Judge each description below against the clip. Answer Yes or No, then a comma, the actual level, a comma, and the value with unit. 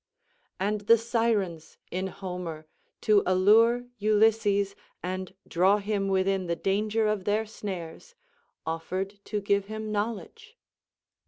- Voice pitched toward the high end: Yes, high, 200 Hz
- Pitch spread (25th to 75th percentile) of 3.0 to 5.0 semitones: No, narrow, 2.5 semitones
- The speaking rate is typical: No, slow, 115 wpm